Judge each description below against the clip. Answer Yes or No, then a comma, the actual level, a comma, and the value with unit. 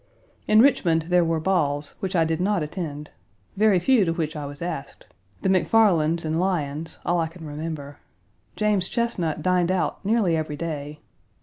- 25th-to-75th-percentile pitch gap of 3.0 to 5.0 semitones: Yes, average, 3.5 semitones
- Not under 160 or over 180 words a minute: Yes, average, 170 wpm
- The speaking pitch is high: No, medium, 165 Hz